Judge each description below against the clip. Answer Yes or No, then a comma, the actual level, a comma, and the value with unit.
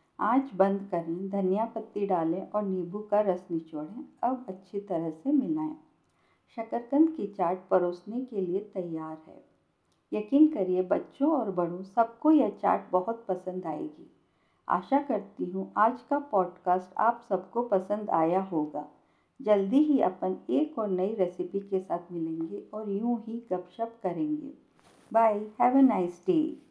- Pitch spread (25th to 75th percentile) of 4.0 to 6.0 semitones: Yes, average, 5.1 semitones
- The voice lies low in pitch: No, high, 205 Hz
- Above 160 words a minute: No, average, 150 wpm